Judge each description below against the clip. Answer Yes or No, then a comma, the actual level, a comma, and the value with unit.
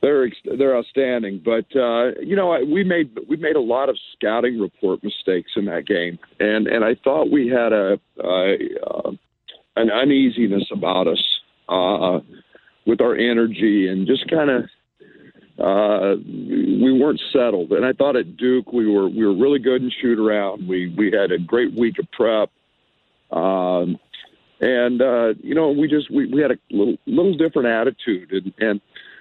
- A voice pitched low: Yes, low, 120 Hz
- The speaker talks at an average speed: Yes, average, 175 wpm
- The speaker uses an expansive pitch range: Yes, wide, 6.7 semitones